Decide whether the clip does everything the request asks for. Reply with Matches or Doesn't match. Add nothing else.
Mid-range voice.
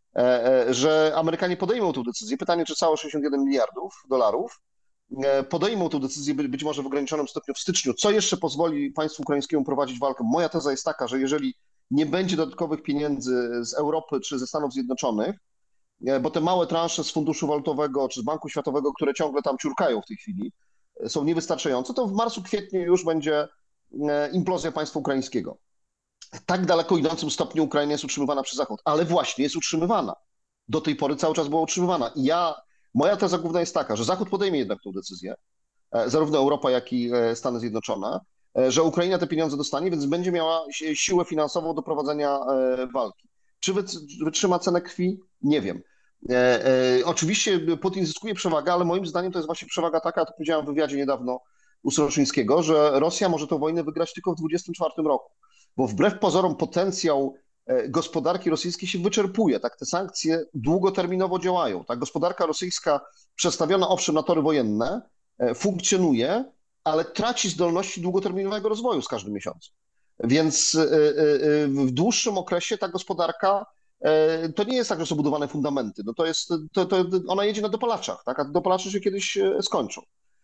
Matches